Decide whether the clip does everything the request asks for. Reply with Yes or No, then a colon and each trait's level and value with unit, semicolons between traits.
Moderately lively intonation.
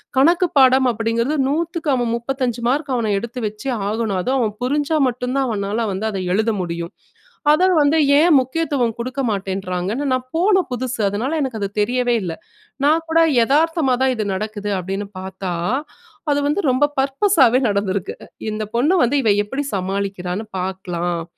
No: wide, 5.9 semitones